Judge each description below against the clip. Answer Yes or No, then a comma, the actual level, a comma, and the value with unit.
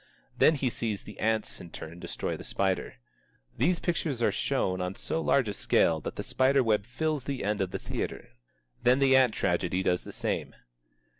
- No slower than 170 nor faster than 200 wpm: Yes, average, 190 wpm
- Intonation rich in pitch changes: Yes, wide, 6.1 semitones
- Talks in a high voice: No, low, 110 Hz